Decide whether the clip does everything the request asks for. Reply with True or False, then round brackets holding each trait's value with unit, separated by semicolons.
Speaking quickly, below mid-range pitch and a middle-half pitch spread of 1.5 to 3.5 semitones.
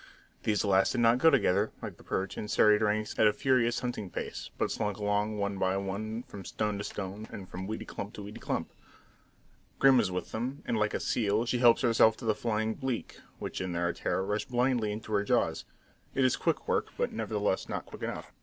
True (220 wpm; 105 Hz; 2.9 semitones)